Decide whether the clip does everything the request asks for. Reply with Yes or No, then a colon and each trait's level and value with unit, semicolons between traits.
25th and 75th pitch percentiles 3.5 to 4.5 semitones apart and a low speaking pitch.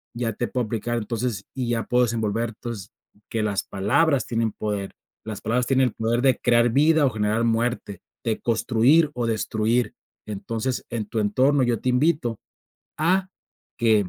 No: narrow, 2.5 semitones; low, 115 Hz